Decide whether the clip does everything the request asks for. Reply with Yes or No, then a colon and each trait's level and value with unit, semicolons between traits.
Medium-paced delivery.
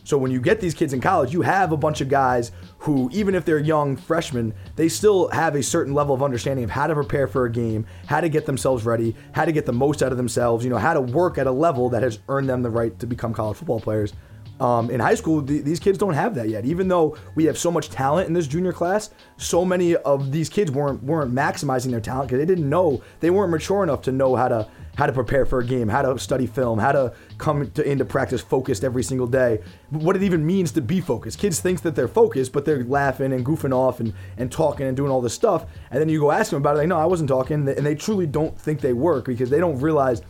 No: fast, 270 wpm